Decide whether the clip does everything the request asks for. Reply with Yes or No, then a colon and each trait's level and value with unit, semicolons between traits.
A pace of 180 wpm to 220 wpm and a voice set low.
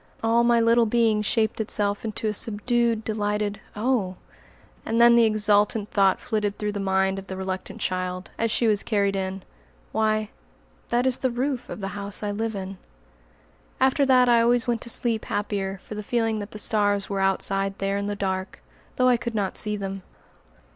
No: average, 190 wpm; high, 210 Hz